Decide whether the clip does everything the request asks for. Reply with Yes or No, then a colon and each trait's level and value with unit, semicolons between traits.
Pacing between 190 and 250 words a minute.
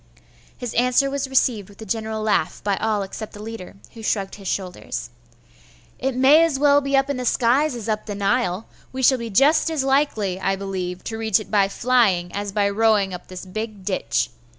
Yes: fast, 205 wpm